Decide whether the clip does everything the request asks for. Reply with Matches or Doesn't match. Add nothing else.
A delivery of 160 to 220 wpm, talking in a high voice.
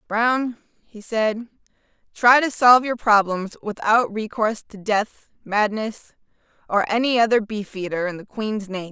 Doesn't match